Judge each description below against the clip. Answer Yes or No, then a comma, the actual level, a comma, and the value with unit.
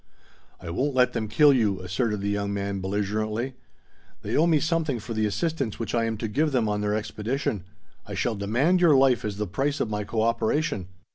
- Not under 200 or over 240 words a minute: Yes, fast, 205 wpm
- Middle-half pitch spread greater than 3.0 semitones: Yes, average, 4.7 semitones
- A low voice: Yes, low, 110 Hz